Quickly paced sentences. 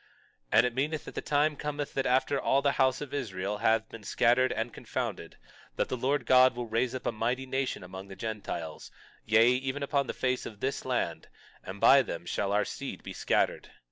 Yes: fast, 210 wpm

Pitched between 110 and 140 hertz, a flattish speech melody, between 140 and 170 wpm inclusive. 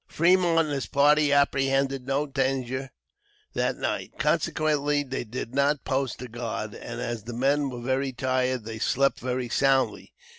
Yes: low, 135 Hz; narrow, 2.1 semitones; average, 155 wpm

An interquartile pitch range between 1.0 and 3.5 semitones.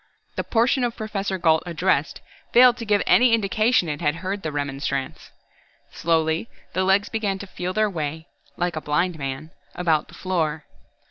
No: average, 4.7 semitones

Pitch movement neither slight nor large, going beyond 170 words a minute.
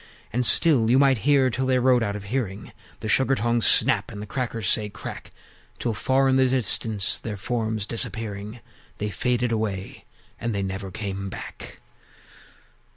No: average, 3.6 semitones; average, 165 wpm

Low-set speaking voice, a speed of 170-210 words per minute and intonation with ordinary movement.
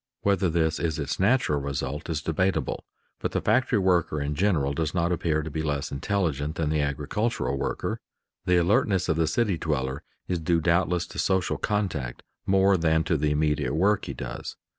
Yes: very low, 80 Hz; average, 185 wpm; average, 4.0 semitones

